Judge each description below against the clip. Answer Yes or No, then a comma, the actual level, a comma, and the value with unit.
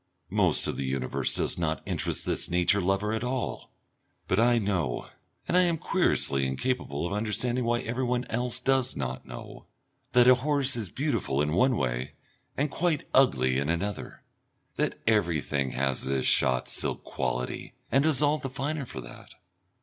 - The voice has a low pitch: Yes, low, 105 Hz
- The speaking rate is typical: Yes, average, 165 wpm